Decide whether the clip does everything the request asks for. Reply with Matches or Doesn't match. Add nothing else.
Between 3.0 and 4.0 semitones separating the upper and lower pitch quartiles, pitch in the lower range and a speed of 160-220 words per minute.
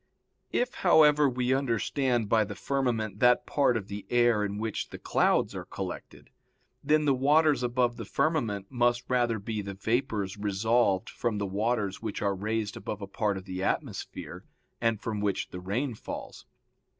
Matches